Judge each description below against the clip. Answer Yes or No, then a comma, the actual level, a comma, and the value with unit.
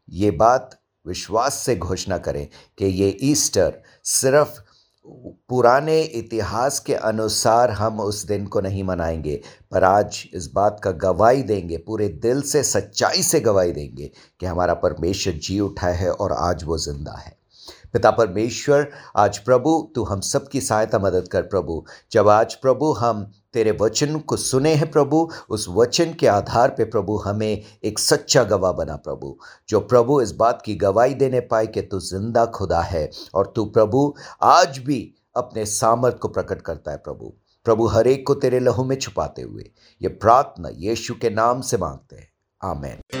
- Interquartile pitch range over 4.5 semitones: Yes, average, 5.0 semitones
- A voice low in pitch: Yes, low, 110 Hz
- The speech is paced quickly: No, average, 170 wpm